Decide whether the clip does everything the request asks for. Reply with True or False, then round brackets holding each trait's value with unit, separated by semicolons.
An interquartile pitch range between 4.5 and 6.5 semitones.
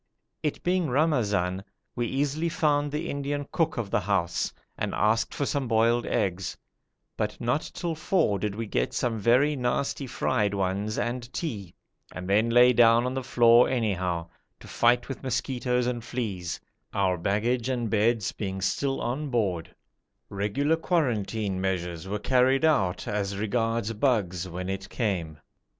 True (5.1 semitones)